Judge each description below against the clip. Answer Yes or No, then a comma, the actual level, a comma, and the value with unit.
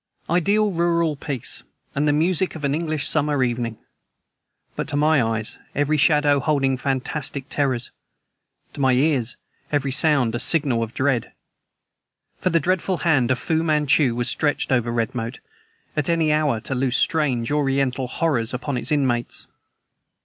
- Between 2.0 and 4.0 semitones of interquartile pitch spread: Yes, average, 3.6 semitones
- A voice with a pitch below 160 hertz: Yes, medium, 140 Hz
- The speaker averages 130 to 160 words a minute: Yes, average, 150 wpm